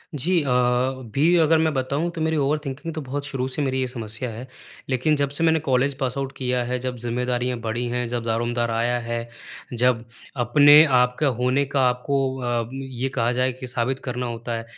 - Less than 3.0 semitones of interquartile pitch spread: Yes, narrow, 2.4 semitones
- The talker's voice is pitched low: Yes, low, 125 Hz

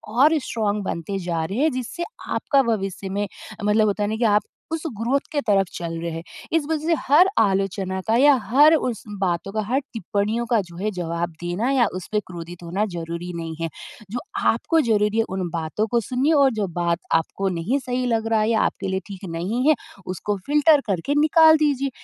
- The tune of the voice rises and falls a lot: Yes, wide, 6.0 semitones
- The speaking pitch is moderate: No, high, 210 Hz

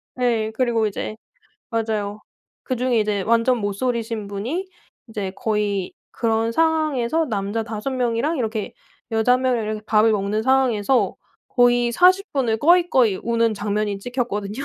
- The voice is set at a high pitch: Yes, high, 230 Hz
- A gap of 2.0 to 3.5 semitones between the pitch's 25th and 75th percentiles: Yes, average, 3.1 semitones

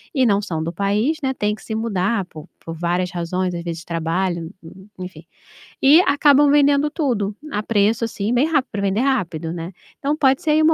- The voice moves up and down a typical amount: No, wide, 7.4 semitones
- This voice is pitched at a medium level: No, high, 205 Hz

